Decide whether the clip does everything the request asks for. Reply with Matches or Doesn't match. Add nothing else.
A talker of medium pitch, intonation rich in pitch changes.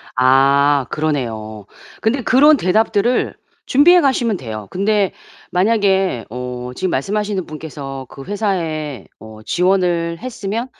Matches